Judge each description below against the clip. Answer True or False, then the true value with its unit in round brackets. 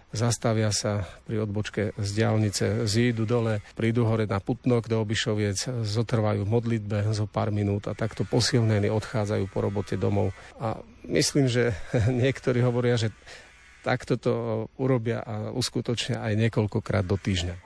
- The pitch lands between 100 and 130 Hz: True (110 Hz)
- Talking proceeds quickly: False (145 wpm)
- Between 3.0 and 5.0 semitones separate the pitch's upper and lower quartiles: False (2.4 semitones)